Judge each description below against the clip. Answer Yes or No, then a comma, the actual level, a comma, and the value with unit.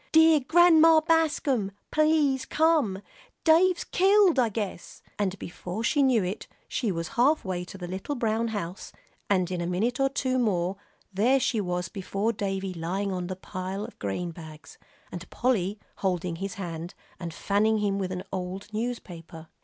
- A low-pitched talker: No, high, 200 Hz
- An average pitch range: No, wide, 6.2 semitones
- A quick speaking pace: No, average, 160 wpm